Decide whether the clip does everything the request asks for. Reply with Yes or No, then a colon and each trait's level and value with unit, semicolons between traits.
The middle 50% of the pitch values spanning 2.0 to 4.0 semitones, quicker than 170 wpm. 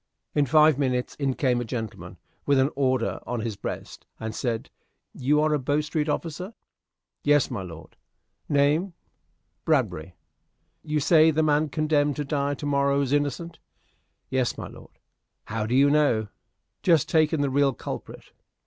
No: average, 3.2 semitones; average, 155 wpm